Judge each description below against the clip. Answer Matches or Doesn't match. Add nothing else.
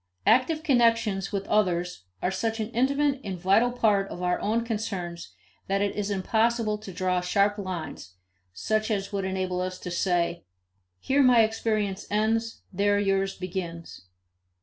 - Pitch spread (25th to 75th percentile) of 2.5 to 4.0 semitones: Matches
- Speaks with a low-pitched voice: Doesn't match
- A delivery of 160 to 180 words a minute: Doesn't match